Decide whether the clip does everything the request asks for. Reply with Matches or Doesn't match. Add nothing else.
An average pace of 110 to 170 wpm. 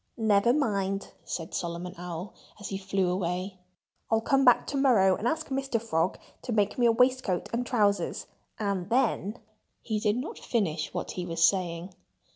Matches